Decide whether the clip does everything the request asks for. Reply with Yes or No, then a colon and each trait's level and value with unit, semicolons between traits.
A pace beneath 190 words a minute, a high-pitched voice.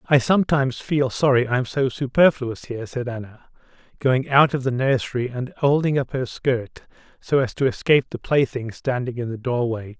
No: average, 180 wpm; low, 130 Hz